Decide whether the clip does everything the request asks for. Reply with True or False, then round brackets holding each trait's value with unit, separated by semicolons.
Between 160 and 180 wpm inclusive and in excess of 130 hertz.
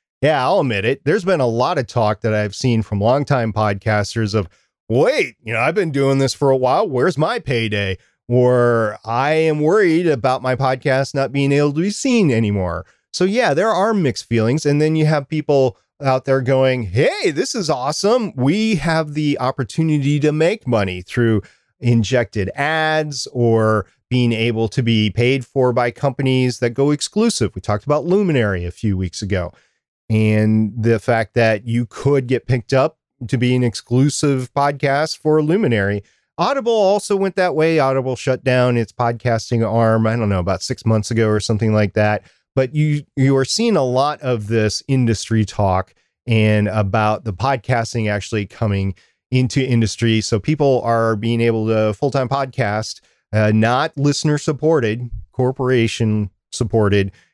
False (170 wpm; 125 Hz)